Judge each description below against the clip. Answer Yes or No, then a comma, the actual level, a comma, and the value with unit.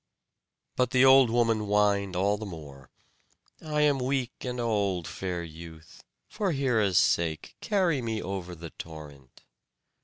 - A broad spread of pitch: Yes, wide, 6.8 semitones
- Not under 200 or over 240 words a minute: No, average, 140 wpm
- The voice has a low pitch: Yes, low, 105 Hz